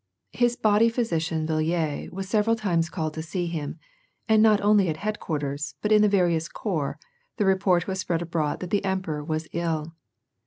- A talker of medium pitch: Yes, medium, 175 Hz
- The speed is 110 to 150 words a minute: No, average, 180 wpm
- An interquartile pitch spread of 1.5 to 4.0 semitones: No, average, 4.6 semitones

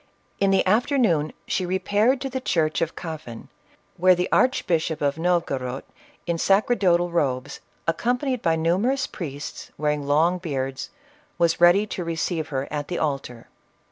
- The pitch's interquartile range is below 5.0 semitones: Yes, average, 4.5 semitones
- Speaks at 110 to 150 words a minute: Yes, average, 145 wpm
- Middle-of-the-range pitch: Yes, medium, 170 Hz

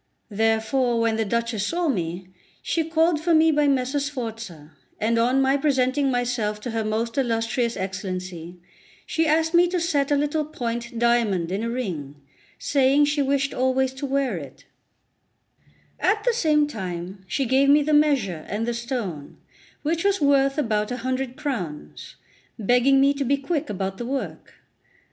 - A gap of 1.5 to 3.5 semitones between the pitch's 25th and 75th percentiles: No, average, 4.8 semitones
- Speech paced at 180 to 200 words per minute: No, average, 165 wpm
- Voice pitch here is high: Yes, very high, 255 Hz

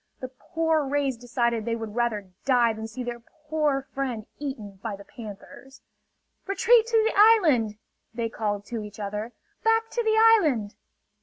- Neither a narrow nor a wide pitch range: No, wide, 5.7 semitones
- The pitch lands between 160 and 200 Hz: No, high, 245 Hz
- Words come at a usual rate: Yes, average, 160 wpm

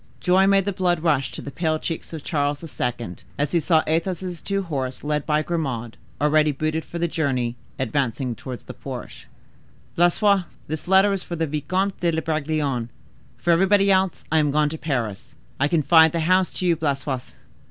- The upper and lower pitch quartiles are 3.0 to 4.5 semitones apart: Yes, average, 3.6 semitones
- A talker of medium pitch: Yes, medium, 160 Hz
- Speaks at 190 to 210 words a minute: No, average, 180 wpm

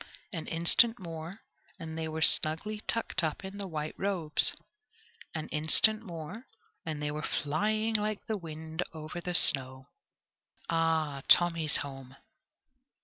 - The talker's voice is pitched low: No, medium, 165 Hz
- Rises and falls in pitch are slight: No, average, 4.2 semitones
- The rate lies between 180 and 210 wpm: No, slow, 135 wpm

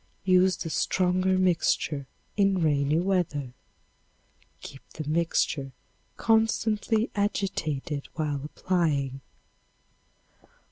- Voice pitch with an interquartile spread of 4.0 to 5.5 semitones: Yes, average, 4.6 semitones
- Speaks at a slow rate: Yes, slow, 80 wpm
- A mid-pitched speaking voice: Yes, medium, 170 Hz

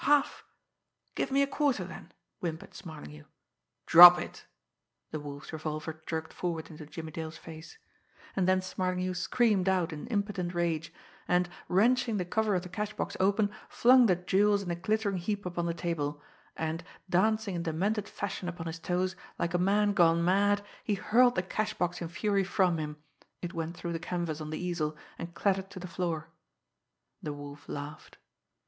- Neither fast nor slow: Yes, average, 175 wpm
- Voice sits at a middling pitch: Yes, medium, 180 Hz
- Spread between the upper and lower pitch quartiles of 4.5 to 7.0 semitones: No, average, 3.6 semitones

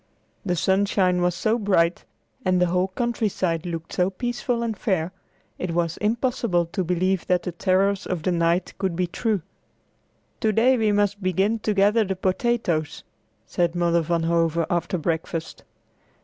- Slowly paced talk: No, average, 160 wpm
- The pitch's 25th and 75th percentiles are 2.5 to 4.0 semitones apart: Yes, average, 3.3 semitones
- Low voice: No, medium, 185 Hz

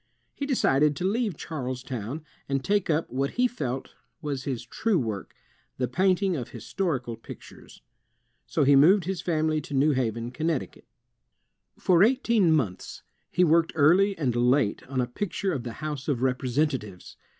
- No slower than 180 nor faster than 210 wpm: No, average, 160 wpm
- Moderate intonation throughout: No, wide, 5.8 semitones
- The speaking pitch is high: No, medium, 145 Hz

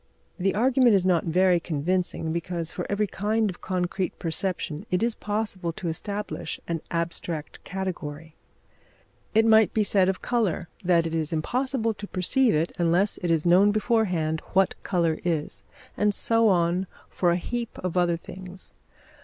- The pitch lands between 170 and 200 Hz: Yes, medium, 185 Hz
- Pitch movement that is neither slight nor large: Yes, average, 3.6 semitones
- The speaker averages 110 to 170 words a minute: Yes, average, 160 wpm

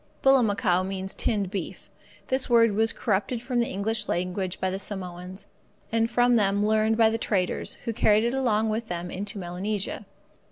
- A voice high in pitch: Yes, high, 210 Hz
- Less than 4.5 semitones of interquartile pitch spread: Yes, average, 3.2 semitones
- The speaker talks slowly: No, average, 170 wpm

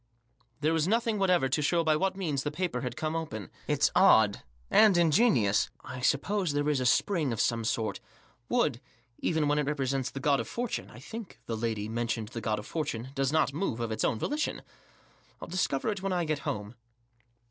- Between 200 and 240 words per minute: Yes, fast, 205 wpm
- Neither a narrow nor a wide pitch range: No, wide, 6.7 semitones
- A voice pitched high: No, medium, 145 Hz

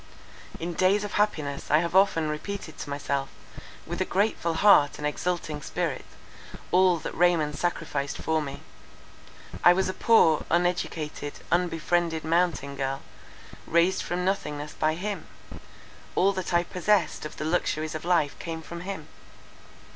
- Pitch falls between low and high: Yes, medium, 170 Hz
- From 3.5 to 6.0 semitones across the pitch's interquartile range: No, average, 3.0 semitones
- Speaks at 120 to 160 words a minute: Yes, average, 145 wpm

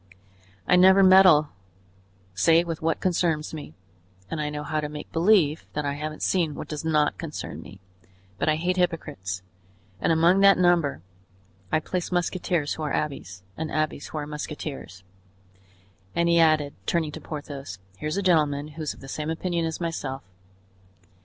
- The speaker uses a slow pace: No, average, 165 wpm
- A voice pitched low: No, medium, 155 Hz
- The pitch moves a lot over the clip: No, narrow, 2.5 semitones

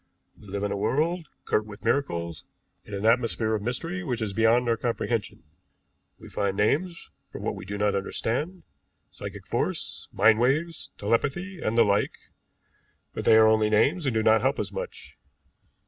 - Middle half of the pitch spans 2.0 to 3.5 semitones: No, average, 5.2 semitones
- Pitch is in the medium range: No, low, 115 Hz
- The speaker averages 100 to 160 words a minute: No, average, 175 wpm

